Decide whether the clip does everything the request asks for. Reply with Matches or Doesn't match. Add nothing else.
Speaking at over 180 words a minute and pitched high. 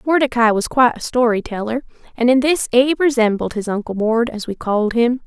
Matches